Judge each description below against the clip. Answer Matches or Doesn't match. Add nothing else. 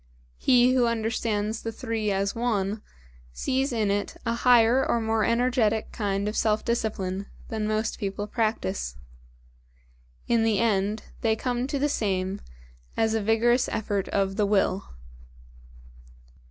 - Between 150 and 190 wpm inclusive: Doesn't match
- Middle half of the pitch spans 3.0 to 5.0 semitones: Doesn't match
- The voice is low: Doesn't match